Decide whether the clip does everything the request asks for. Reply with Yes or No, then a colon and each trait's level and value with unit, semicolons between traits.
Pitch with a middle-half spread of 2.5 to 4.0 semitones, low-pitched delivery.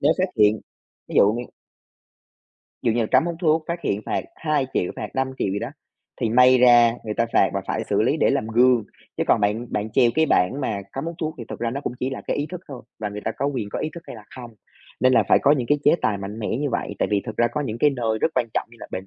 No: average, 4.5 semitones; low, 120 Hz